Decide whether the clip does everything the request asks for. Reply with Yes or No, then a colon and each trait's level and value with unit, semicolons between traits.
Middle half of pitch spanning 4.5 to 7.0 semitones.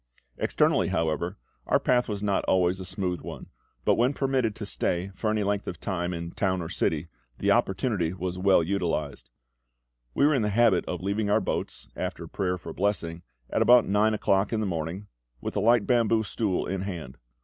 No: average, 3.5 semitones